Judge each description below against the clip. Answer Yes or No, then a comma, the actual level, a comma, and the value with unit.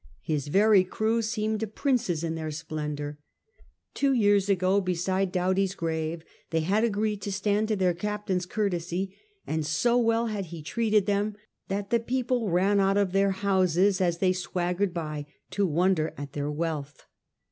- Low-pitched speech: No, high, 190 Hz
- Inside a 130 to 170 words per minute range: Yes, average, 160 wpm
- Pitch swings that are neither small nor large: Yes, average, 3.8 semitones